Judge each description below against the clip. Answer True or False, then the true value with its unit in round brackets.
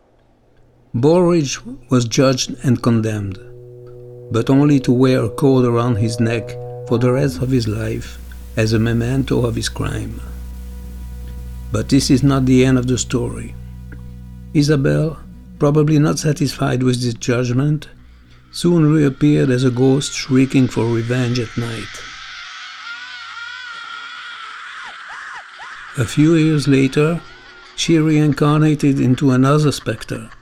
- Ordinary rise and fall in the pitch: True (4.4 semitones)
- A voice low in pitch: True (125 Hz)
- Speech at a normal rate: False (120 wpm)